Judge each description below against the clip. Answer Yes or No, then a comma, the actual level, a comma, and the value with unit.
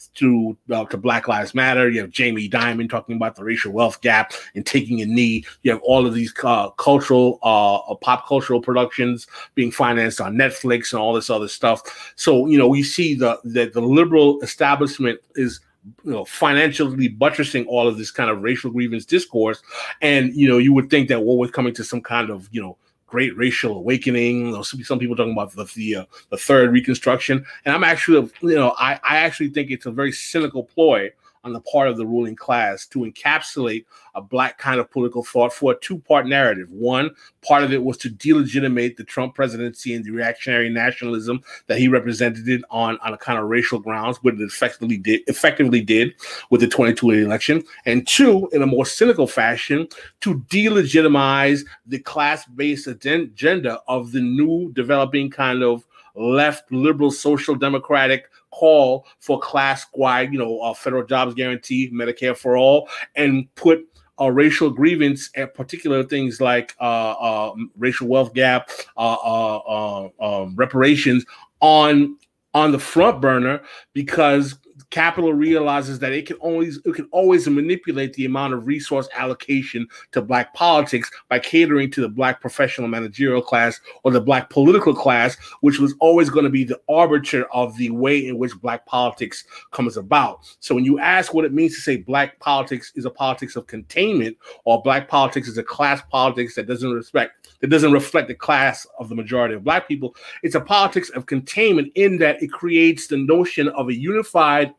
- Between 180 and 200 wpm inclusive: Yes, average, 185 wpm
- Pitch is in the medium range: No, low, 130 Hz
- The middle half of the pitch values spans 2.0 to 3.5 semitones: Yes, average, 3.1 semitones